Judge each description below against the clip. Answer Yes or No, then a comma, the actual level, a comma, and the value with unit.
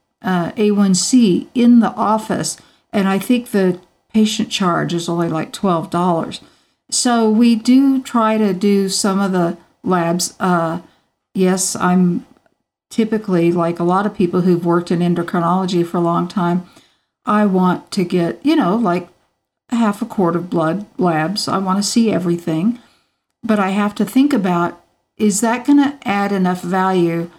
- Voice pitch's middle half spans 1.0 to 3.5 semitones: No, average, 4.0 semitones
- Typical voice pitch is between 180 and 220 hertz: Yes, high, 190 Hz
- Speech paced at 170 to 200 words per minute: No, average, 160 wpm